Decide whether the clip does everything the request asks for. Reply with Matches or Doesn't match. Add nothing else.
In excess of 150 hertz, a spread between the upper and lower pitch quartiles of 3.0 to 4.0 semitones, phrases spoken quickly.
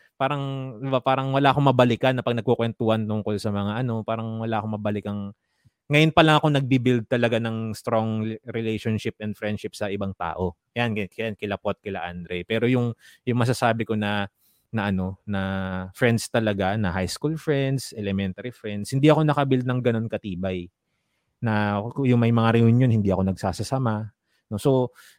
Doesn't match